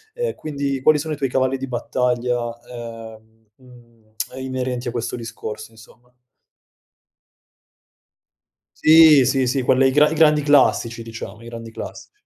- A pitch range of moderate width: Yes, average, 3.0 semitones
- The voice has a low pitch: Yes, low, 125 Hz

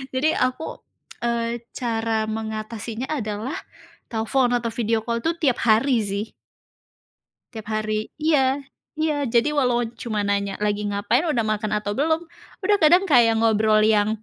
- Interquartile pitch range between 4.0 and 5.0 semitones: No, average, 3.6 semitones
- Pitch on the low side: No, high, 230 Hz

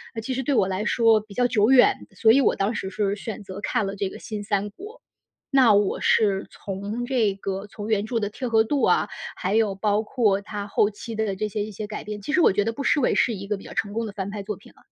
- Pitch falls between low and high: No, high, 210 Hz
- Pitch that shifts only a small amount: Yes, narrow, 2.2 semitones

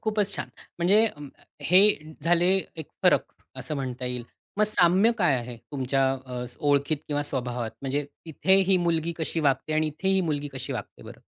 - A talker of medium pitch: Yes, medium, 150 Hz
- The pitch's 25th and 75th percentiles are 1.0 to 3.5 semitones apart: No, average, 4.8 semitones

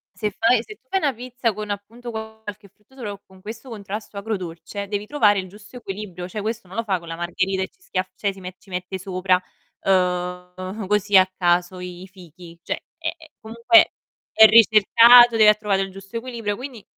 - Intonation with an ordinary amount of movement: Yes, average, 3.3 semitones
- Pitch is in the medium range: No, high, 205 Hz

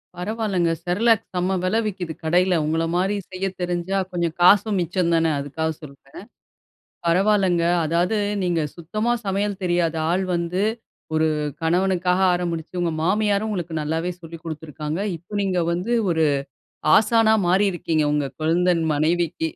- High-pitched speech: No, medium, 175 Hz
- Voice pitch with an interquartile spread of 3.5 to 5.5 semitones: No, average, 2.8 semitones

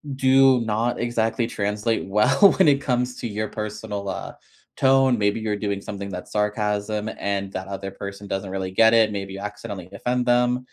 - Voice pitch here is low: Yes, low, 105 Hz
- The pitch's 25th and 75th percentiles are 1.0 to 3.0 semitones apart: No, average, 3.4 semitones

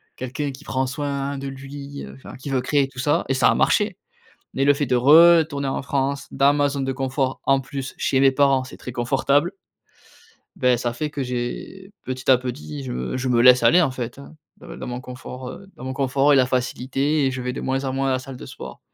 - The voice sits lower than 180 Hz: Yes, low, 135 Hz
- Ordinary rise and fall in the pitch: No, narrow, 1.8 semitones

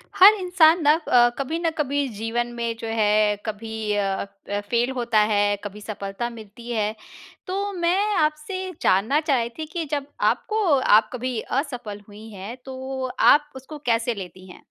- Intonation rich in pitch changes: Yes, wide, 6.1 semitones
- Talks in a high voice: Yes, high, 240 Hz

